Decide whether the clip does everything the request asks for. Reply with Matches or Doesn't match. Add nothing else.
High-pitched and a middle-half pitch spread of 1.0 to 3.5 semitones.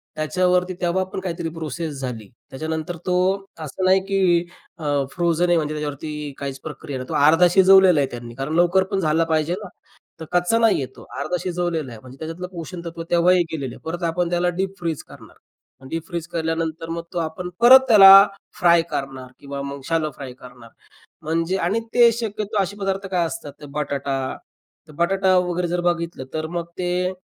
Doesn't match